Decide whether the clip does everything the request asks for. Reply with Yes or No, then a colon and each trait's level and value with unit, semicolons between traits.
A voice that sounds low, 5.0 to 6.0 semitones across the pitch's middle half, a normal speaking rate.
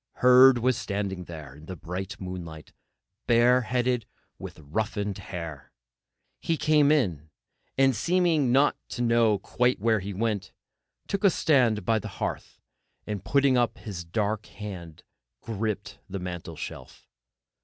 No: low, 110 Hz; average, 5.3 semitones; slow, 130 wpm